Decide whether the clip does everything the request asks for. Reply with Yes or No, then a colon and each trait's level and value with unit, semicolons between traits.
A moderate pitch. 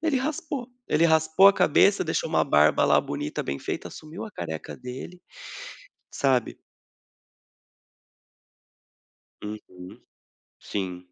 Yes: medium, 155 Hz